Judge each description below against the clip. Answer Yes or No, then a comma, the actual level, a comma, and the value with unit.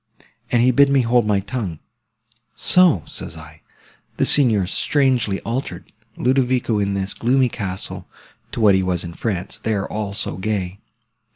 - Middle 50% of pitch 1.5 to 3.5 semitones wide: No, average, 4.6 semitones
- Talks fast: No, average, 155 wpm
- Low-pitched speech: Yes, low, 110 Hz